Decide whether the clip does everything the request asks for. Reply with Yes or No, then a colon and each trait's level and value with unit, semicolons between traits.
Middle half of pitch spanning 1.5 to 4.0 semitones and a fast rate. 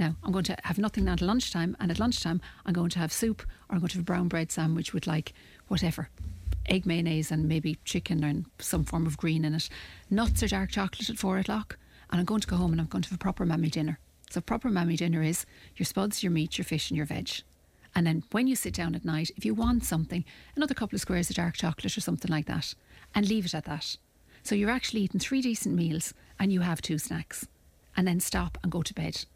Yes: average, 3.5 semitones; fast, 255 wpm